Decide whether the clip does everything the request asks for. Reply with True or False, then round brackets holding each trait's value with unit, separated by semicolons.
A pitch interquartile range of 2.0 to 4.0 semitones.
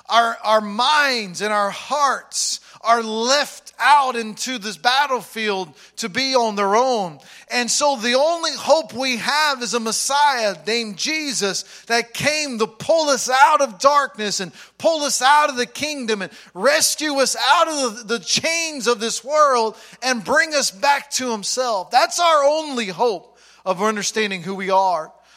False (4.8 semitones)